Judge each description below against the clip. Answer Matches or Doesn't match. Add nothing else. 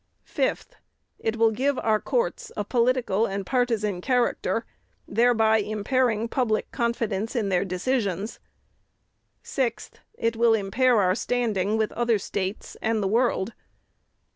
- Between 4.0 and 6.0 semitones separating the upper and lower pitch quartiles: Doesn't match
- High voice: Matches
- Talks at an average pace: Doesn't match